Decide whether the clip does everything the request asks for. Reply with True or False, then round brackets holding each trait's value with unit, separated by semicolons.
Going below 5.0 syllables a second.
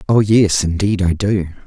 True (4.4 syllables/s)